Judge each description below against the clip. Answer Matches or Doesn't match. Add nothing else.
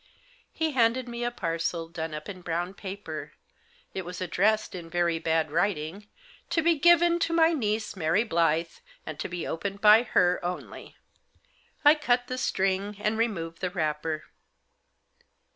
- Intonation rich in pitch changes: Matches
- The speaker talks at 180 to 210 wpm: Doesn't match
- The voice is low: Doesn't match